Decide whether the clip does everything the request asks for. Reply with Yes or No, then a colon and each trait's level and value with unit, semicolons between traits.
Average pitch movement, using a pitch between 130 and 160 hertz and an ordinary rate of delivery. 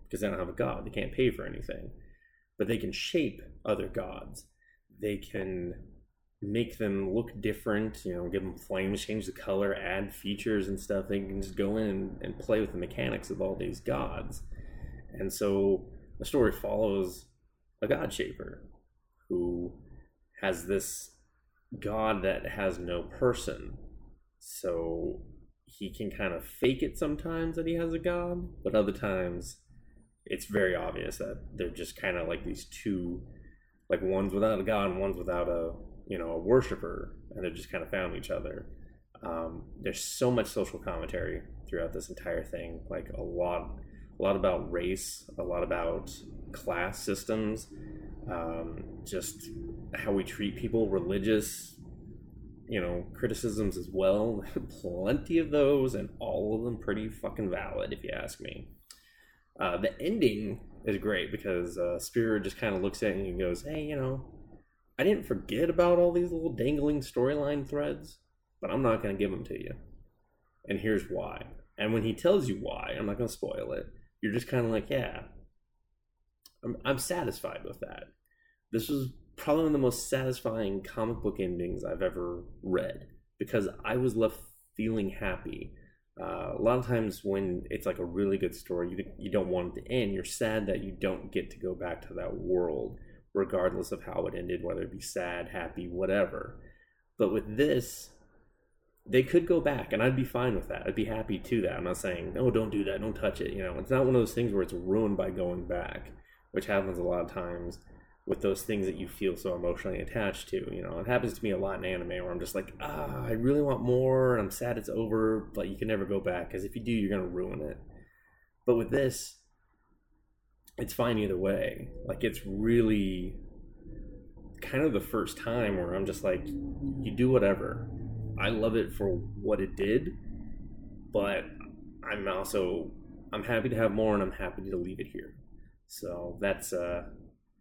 No: average, 4.2 semitones; low, 105 Hz; average, 185 wpm